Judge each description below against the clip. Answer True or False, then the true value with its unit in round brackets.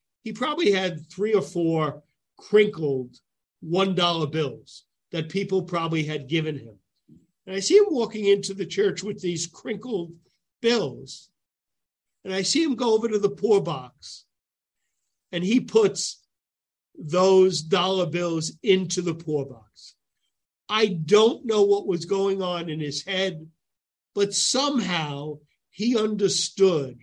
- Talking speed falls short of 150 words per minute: True (135 wpm)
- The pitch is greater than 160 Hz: True (185 Hz)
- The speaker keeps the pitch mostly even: False (4.5 semitones)